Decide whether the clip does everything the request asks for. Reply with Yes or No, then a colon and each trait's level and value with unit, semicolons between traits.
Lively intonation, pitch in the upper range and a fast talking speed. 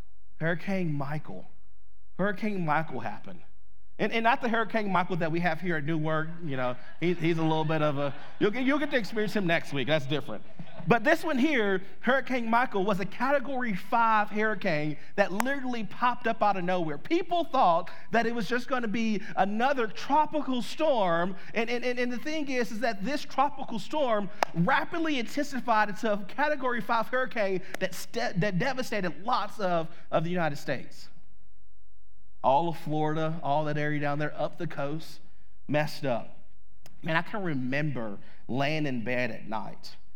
No: wide, 7.5 semitones; high, 195 Hz; average, 175 wpm